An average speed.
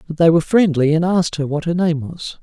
No: fast, 275 wpm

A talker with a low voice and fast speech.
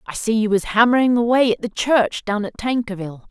No: high, 220 Hz; fast, 220 wpm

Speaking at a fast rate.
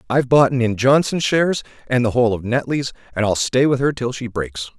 Yes: fast, 225 wpm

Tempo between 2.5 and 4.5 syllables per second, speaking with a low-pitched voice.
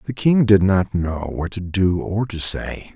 Yes: 4.0 syllables/s; low, 100 Hz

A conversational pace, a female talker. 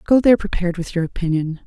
No: fast, 215 wpm; female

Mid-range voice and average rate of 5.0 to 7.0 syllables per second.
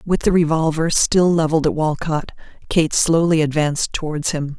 Yes: medium, 160 Hz; 5.1 syllables/s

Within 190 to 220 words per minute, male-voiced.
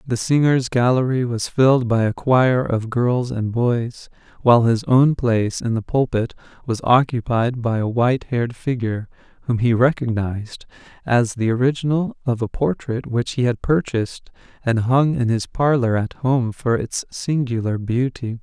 No: average, 165 wpm; male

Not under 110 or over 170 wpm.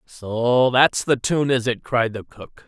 No: average, 200 wpm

